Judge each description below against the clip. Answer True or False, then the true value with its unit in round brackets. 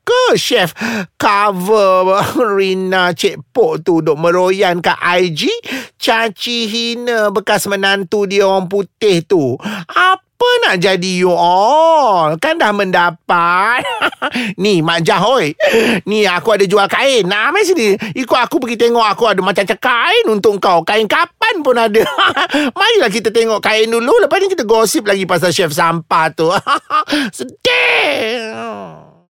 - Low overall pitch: False (220 Hz)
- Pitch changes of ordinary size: False (6.6 semitones)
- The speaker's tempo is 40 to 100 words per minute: False (135 wpm)